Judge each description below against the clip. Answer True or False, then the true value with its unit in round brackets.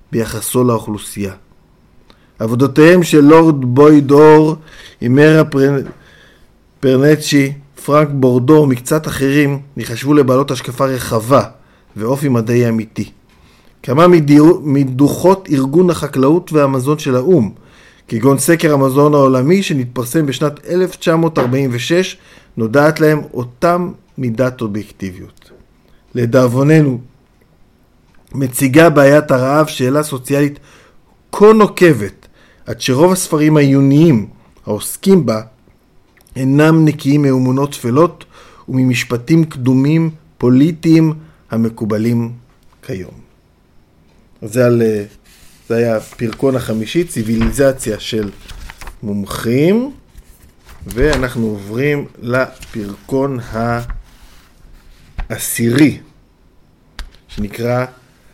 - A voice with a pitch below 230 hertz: True (135 Hz)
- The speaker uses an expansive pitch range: False (4.8 semitones)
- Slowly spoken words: True (75 wpm)